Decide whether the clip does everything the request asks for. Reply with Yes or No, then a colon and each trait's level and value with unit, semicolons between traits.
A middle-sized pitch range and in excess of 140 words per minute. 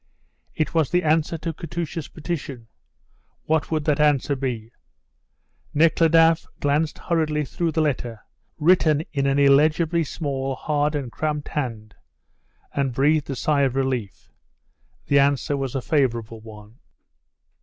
No: average, 3.0 semitones; slow, 135 wpm